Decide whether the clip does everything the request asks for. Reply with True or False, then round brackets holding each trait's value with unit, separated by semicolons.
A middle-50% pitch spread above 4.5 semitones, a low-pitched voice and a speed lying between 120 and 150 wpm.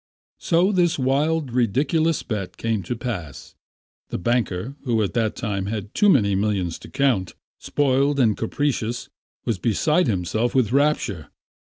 True (5.5 semitones; 120 Hz; 140 wpm)